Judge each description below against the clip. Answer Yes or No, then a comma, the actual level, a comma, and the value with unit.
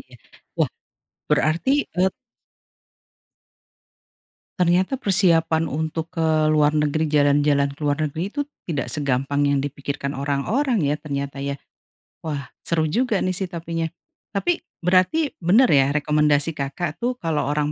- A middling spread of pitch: Yes, average, 3.7 semitones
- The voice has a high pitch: No, medium, 155 Hz